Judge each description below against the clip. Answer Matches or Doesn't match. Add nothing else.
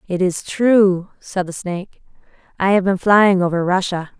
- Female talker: Matches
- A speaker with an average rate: Matches